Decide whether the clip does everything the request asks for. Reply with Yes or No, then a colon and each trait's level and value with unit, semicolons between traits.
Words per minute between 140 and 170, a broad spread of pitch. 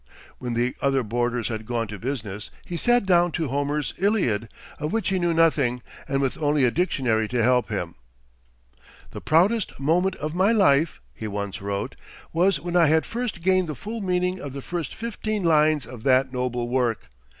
No: average, 185 wpm; wide, 6.6 semitones